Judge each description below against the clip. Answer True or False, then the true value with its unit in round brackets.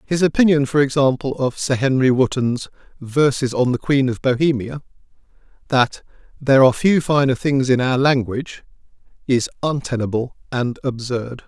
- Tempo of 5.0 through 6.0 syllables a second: True (5.1 syllables/s)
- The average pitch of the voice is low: True (130 Hz)